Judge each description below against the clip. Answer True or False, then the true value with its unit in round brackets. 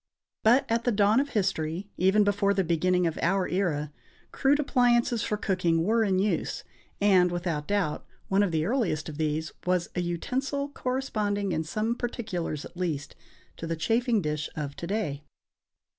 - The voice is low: False (190 Hz)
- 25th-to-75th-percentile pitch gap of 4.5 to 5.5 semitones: True (5.2 semitones)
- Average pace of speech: True (170 wpm)